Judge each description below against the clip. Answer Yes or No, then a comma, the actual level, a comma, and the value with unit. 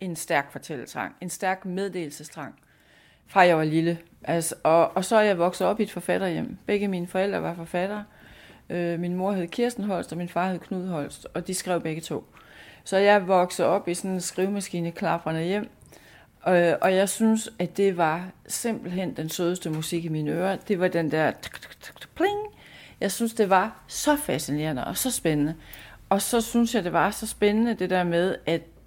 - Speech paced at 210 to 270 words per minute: No, average, 195 wpm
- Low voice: No, medium, 180 Hz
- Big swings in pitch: No, average, 3.2 semitones